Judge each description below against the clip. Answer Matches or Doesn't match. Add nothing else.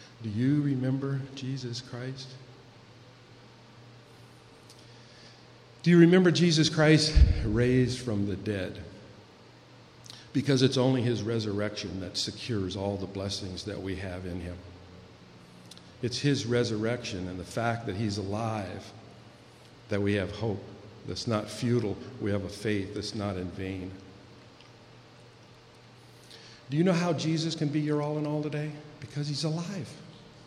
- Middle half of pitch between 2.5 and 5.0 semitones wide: Matches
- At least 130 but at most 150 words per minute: Matches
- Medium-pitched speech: Doesn't match